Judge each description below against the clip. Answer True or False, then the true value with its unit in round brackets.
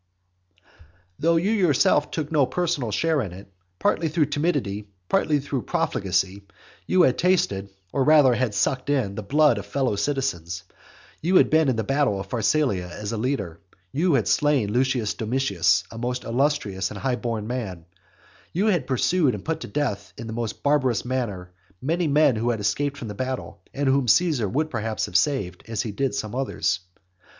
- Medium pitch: False (125 Hz)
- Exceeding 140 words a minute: True (185 wpm)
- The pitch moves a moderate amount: False (6.3 semitones)